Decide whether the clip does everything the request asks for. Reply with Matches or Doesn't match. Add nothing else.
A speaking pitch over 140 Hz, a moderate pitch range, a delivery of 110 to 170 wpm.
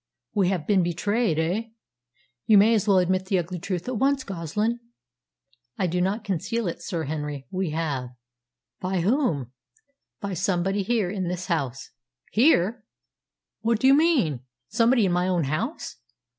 Matches